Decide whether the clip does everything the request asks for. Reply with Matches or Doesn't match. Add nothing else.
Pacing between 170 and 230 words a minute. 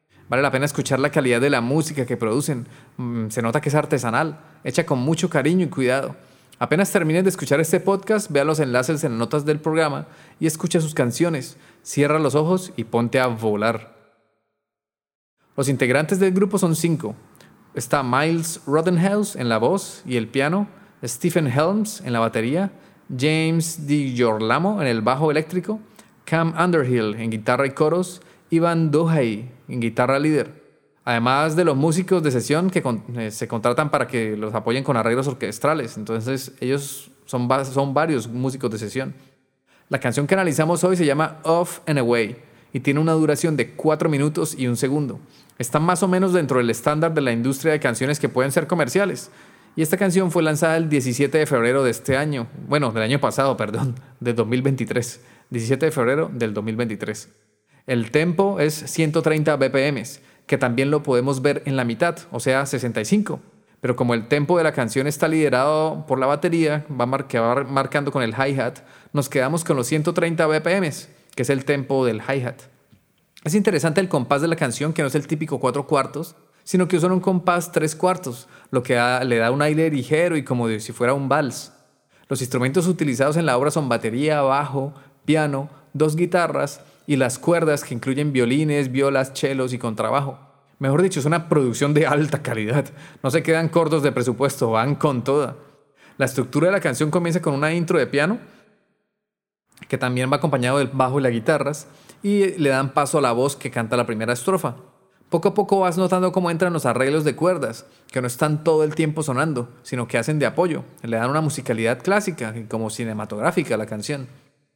Matches